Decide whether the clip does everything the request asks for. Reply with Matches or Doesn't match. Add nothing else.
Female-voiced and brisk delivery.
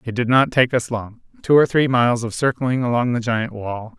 Doesn't match